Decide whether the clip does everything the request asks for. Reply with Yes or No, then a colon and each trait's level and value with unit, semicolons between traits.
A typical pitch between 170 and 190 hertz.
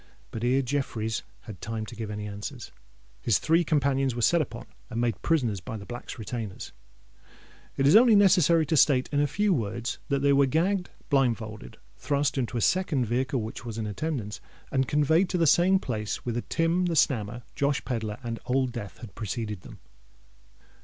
No: low, 130 Hz